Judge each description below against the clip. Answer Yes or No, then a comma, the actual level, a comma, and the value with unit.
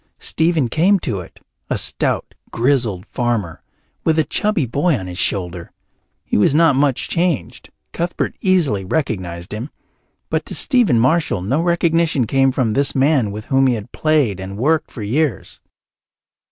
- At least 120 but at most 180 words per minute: Yes, average, 155 wpm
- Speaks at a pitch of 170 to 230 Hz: No, low, 135 Hz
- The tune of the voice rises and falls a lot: Yes, wide, 7.3 semitones